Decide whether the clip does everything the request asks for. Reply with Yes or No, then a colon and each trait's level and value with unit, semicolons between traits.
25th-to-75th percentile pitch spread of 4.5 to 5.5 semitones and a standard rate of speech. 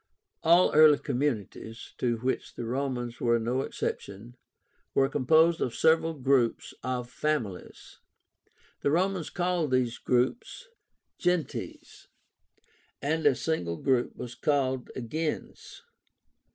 No: average, 4.8 semitones; slow, 110 wpm